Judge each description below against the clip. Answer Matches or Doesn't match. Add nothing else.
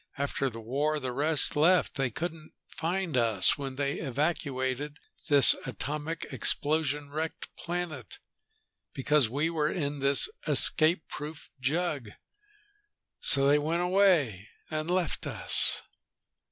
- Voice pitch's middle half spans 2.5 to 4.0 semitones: Matches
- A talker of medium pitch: Matches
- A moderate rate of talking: Doesn't match